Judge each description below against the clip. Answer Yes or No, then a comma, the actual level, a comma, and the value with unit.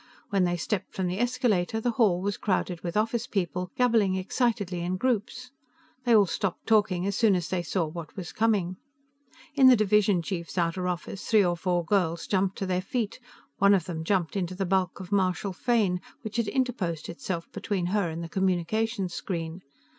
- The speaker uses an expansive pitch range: No, average, 3.3 semitones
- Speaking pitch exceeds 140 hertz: Yes, high, 190 Hz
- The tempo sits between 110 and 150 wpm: No, average, 190 wpm